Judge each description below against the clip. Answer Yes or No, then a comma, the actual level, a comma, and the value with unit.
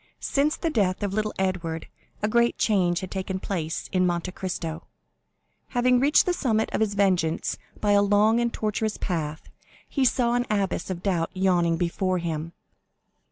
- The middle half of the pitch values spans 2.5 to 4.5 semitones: Yes, average, 3.9 semitones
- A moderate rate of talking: Yes, average, 165 wpm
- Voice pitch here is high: Yes, high, 195 Hz